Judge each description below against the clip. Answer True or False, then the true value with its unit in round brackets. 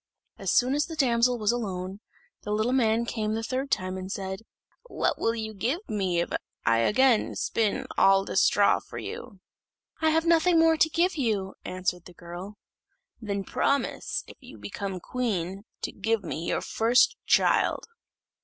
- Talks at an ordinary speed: True (170 wpm)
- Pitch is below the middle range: False (220 Hz)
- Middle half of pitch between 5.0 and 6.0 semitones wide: True (5.3 semitones)